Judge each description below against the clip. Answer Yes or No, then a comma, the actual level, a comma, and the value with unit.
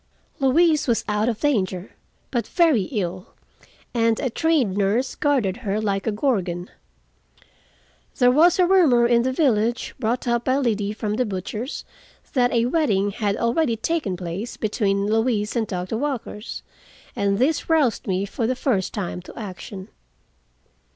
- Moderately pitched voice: No, high, 230 Hz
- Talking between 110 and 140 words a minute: No, average, 150 wpm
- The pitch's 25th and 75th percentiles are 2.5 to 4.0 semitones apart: No, average, 4.4 semitones